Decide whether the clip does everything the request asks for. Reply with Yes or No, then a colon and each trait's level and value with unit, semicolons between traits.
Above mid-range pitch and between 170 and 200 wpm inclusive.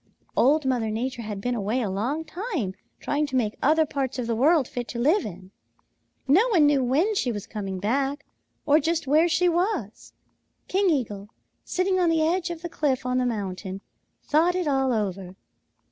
Yes: very high, 270 Hz; average, 190 wpm